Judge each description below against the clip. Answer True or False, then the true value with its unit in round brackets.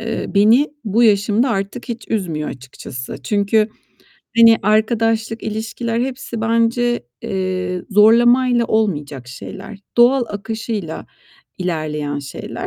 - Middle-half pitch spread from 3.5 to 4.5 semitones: True (3.9 semitones)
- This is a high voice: True (215 Hz)